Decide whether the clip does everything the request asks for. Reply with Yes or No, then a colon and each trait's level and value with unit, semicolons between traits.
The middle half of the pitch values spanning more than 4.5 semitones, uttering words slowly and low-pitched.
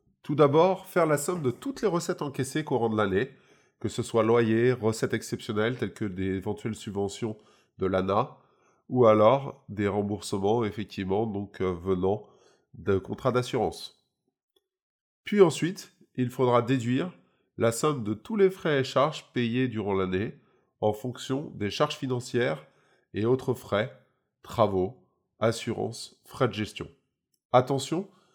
Yes: average, 5.1 semitones; slow, 140 wpm; low, 120 Hz